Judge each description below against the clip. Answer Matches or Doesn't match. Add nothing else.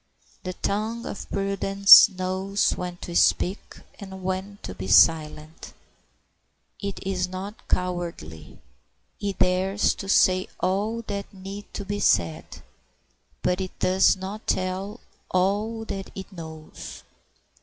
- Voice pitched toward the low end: Doesn't match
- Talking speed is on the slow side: Matches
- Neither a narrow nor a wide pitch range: Doesn't match